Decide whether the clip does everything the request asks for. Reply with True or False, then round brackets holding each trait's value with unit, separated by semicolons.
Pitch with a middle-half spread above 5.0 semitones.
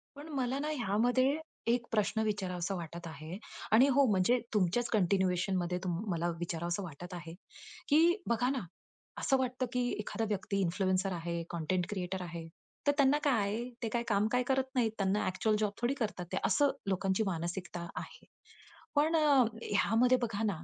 True (5.5 semitones)